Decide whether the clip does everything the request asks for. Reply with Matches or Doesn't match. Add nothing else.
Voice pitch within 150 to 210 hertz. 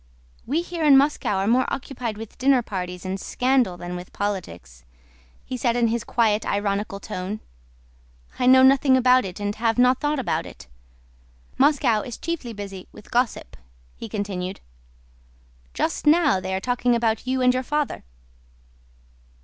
Doesn't match